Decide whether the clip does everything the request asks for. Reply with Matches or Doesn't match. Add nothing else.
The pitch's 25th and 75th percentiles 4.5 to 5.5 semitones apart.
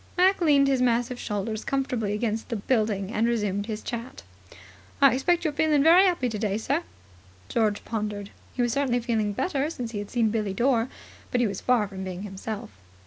Doesn't match